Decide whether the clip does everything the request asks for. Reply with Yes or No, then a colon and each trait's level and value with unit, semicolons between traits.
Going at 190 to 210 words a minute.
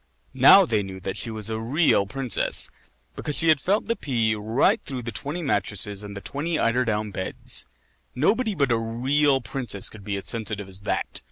Yes: average, 195 wpm